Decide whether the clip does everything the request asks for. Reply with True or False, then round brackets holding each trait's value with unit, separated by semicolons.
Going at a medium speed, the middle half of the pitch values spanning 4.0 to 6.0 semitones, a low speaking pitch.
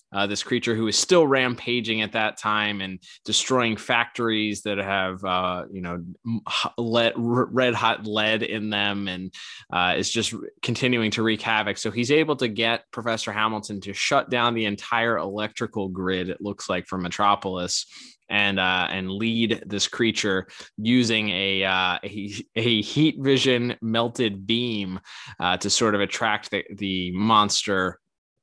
False (155 wpm; 2.9 semitones; 110 Hz)